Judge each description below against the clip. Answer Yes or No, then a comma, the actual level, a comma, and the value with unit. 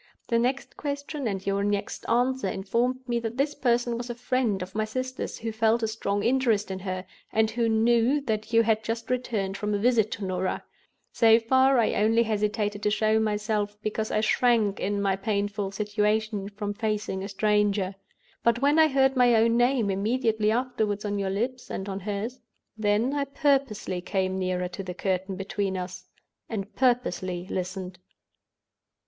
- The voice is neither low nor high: No, high, 215 Hz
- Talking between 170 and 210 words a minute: Yes, average, 175 wpm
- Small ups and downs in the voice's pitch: No, average, 3.2 semitones